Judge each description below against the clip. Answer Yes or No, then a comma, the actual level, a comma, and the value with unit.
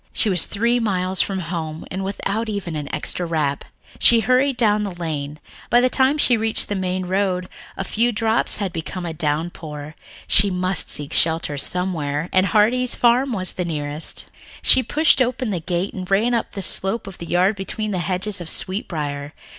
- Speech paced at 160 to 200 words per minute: Yes, average, 190 wpm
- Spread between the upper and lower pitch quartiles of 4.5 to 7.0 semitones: Yes, average, 4.8 semitones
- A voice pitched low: No, high, 190 Hz